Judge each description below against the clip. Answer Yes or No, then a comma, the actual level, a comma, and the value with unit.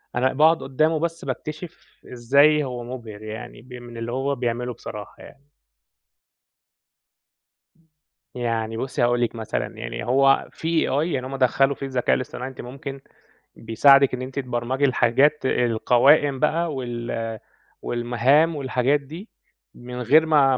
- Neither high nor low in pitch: No, low, 130 Hz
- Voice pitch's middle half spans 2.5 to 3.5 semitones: Yes, average, 2.9 semitones